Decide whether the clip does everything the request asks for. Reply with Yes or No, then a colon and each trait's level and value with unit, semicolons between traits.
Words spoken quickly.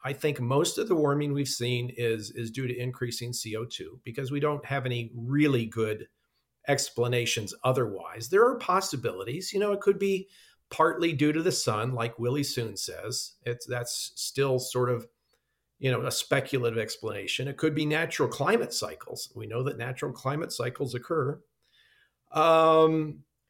No: average, 165 wpm